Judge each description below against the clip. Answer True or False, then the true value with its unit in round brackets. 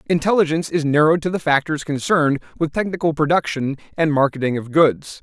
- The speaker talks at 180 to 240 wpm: False (160 wpm)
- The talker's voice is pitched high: False (155 Hz)